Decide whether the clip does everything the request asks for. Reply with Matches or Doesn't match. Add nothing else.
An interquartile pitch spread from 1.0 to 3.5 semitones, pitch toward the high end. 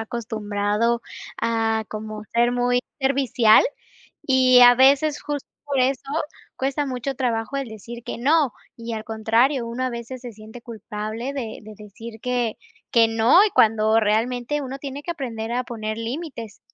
Matches